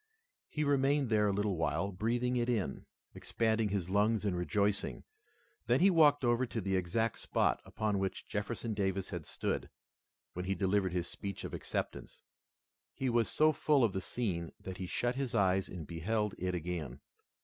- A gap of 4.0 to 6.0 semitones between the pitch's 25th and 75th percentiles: Yes, average, 4.3 semitones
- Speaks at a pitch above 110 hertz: No, low, 105 Hz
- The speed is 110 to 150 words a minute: No, average, 175 wpm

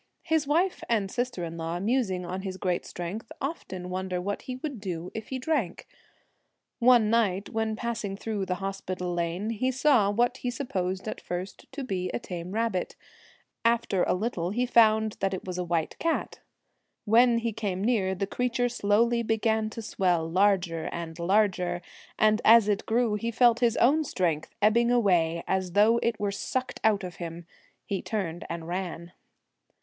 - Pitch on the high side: Yes, high, 205 Hz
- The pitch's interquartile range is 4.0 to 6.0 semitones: Yes, average, 4.5 semitones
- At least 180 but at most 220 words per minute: Yes, average, 185 wpm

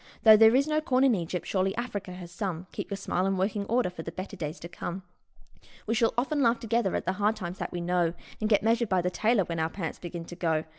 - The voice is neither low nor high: No, high, 195 Hz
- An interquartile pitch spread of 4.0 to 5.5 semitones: Yes, average, 4.3 semitones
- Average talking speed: No, fast, 260 wpm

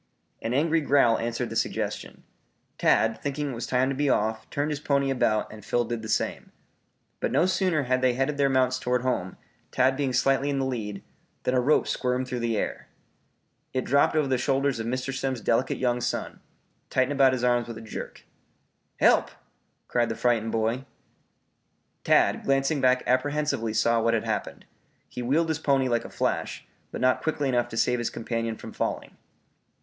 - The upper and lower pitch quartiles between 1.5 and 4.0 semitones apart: Yes, average, 2.7 semitones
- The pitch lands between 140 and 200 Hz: No, low, 130 Hz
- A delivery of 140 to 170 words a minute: No, average, 190 wpm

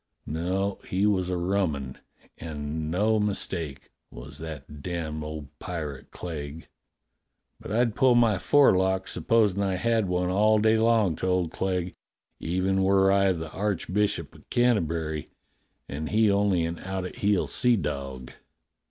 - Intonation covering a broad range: No, average, 4.3 semitones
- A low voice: Yes, very low, 90 Hz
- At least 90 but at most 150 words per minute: Yes, average, 140 wpm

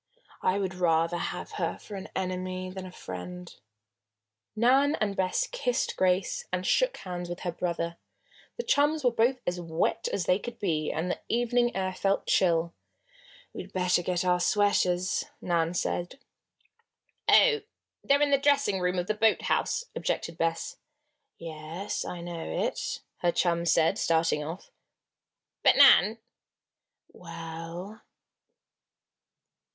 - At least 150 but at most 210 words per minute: No, slow, 135 wpm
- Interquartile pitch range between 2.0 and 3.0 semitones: No, average, 4.3 semitones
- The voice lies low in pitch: No, medium, 185 Hz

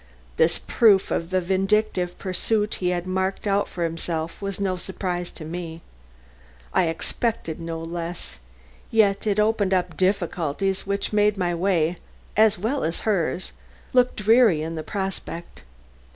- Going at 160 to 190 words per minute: No, average, 145 wpm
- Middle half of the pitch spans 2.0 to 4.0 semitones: Yes, average, 3.1 semitones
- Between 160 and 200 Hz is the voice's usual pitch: Yes, medium, 185 Hz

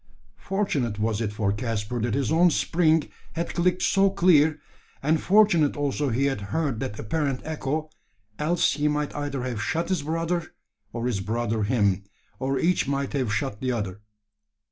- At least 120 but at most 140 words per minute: No, average, 165 wpm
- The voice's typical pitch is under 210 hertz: Yes, medium, 140 Hz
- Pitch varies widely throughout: Yes, wide, 6.0 semitones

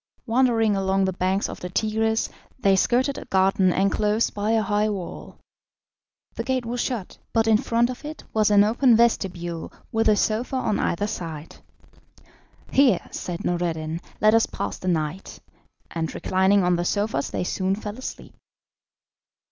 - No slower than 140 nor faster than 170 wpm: Yes, average, 160 wpm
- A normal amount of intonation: Yes, average, 3.4 semitones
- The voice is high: Yes, high, 205 Hz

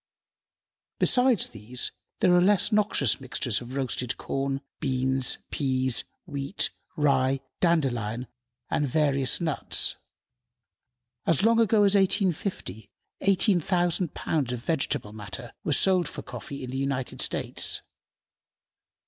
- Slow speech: Yes, slow, 110 wpm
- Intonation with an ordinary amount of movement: No, wide, 5.7 semitones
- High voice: No, medium, 140 Hz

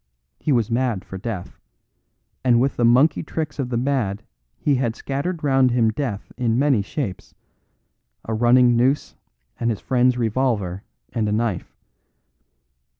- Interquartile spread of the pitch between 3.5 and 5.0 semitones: No, average, 3.1 semitones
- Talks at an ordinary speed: Yes, average, 150 wpm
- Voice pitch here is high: No, low, 120 Hz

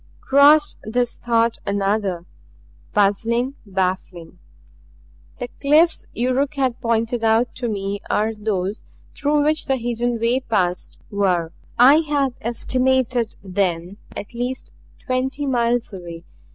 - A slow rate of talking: Yes, slow, 115 wpm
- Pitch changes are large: No, average, 4.5 semitones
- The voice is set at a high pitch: Yes, high, 235 Hz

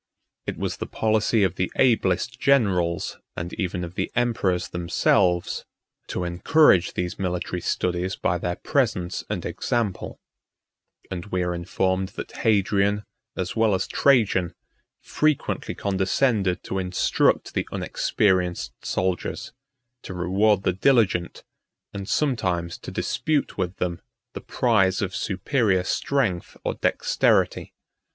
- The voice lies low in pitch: Yes, very low, 95 Hz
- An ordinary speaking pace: No, slow, 125 wpm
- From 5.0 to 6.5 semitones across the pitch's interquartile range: No, average, 3.5 semitones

